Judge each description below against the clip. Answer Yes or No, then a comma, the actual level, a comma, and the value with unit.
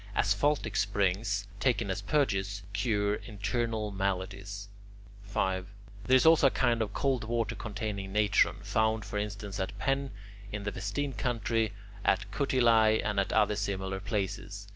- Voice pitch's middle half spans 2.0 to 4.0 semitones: Yes, narrow, 2.4 semitones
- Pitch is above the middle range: No, low, 105 Hz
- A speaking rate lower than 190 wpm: Yes, average, 140 wpm